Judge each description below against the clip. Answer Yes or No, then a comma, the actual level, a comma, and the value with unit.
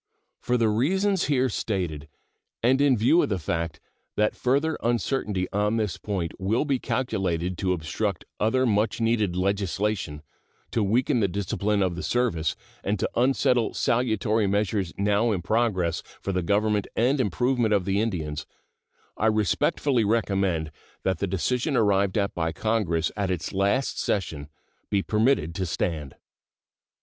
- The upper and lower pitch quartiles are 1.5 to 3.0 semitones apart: No, average, 4.1 semitones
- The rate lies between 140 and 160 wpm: Yes, average, 150 wpm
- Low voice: Yes, low, 105 Hz